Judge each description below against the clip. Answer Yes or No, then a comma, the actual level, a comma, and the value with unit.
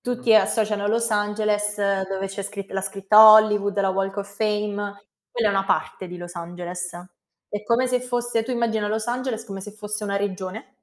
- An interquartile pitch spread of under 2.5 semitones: Yes, narrow, 2.1 semitones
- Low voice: No, high, 210 Hz